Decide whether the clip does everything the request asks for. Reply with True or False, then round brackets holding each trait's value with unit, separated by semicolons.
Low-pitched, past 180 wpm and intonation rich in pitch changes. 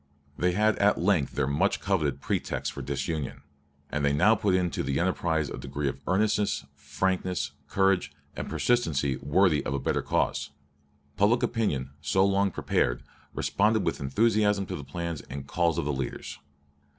False (85 Hz; 165 wpm; 6.1 semitones)